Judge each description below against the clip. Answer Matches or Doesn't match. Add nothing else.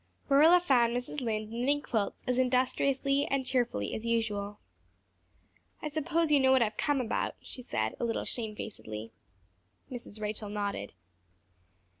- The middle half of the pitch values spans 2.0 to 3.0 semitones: Doesn't match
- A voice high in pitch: Matches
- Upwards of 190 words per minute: Doesn't match